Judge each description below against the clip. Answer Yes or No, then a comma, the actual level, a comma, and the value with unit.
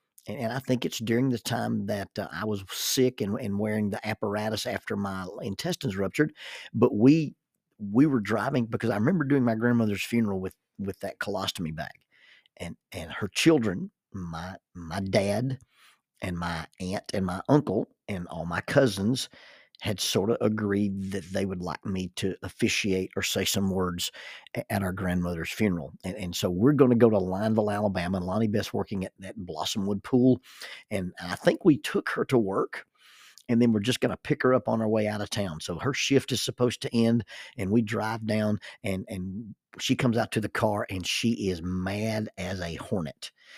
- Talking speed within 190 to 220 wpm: Yes, average, 195 wpm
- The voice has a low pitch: Yes, low, 105 Hz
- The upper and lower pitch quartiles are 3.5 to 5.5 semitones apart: Yes, average, 3.8 semitones